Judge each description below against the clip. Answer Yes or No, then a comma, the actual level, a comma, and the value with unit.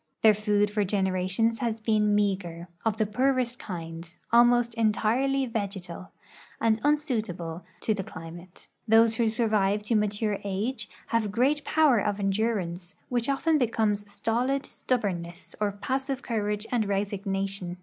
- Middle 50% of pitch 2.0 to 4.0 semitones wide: Yes, average, 3.2 semitones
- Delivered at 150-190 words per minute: No, average, 140 wpm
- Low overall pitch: No, high, 210 Hz